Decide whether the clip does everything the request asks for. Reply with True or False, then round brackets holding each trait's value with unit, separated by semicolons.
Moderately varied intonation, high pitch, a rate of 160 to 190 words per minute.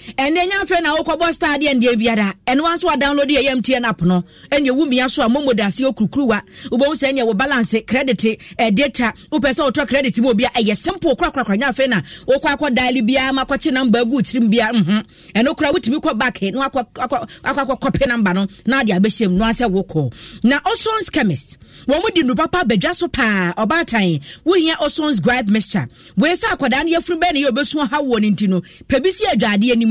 True (4.8 semitones; 255 Hz; 180 wpm)